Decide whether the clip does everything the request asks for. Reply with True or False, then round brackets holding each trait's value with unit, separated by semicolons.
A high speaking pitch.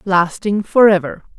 True (195 Hz)